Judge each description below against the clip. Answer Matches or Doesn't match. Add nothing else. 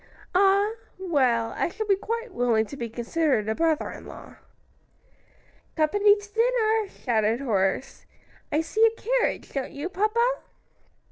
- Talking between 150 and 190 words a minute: Doesn't match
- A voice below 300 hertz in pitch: Doesn't match